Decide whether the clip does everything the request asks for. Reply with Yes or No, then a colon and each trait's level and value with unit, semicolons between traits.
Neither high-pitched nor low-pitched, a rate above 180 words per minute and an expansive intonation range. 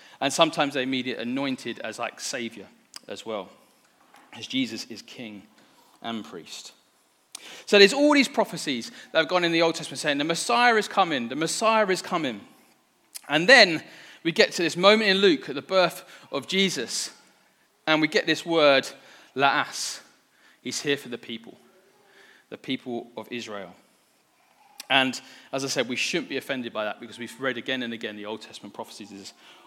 No: medium, 155 Hz; average, 175 wpm; wide, 7.2 semitones